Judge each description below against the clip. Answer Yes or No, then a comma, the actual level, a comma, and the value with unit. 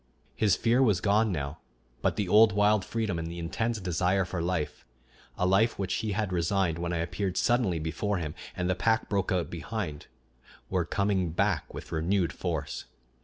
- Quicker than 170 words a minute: Yes, average, 180 wpm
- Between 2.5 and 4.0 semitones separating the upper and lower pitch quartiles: Yes, average, 3.6 semitones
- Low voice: Yes, very low, 95 Hz